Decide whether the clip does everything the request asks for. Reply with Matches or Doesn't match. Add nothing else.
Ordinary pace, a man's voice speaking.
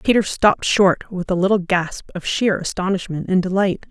Doesn't match